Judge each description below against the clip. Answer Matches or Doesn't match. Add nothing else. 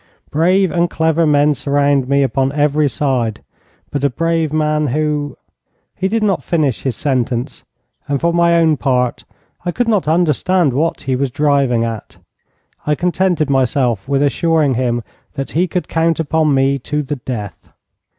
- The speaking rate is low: Doesn't match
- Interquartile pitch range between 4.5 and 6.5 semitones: Doesn't match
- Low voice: Doesn't match